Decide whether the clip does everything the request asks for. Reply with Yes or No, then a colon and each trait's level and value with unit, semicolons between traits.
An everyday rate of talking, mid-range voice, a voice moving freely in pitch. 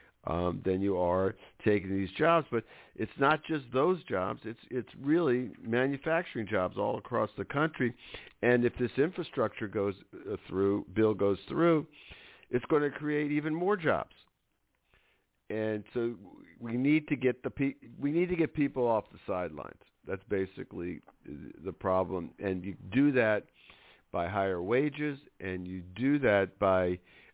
No: average, 155 wpm; low, 120 Hz; wide, 7.0 semitones